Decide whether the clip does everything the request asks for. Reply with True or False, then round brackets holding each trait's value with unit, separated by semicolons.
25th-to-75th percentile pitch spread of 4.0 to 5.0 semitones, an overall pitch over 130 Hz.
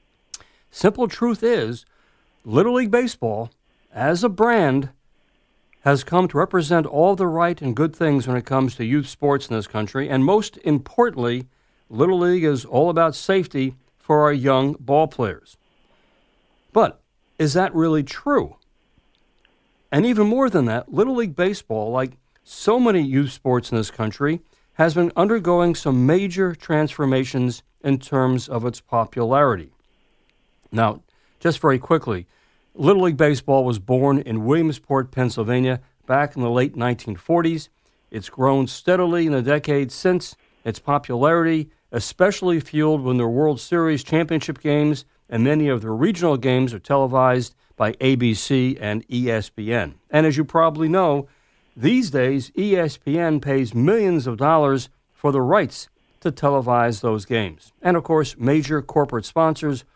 True (4.7 semitones; 140 Hz)